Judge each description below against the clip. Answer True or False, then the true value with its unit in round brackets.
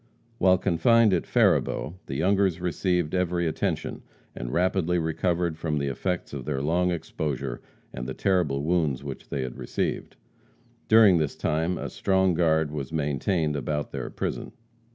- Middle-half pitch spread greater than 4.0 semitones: False (3.7 semitones)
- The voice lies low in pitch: True (80 Hz)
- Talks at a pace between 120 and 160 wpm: True (155 wpm)